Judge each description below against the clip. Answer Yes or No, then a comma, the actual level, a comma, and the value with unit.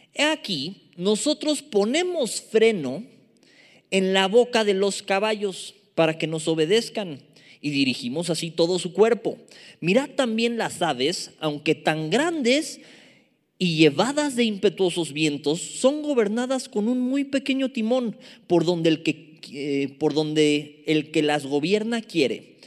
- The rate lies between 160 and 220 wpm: No, average, 135 wpm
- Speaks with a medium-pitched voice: No, high, 200 Hz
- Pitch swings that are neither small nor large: No, wide, 7.7 semitones